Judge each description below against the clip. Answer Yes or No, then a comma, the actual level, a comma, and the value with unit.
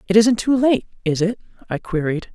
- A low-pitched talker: No, high, 205 Hz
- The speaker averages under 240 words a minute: Yes, fast, 205 wpm